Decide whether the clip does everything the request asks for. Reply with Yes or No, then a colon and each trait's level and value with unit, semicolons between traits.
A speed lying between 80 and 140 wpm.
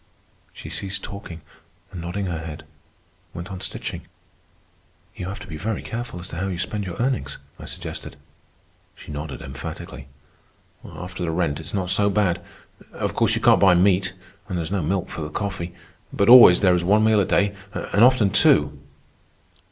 No: average, 185 wpm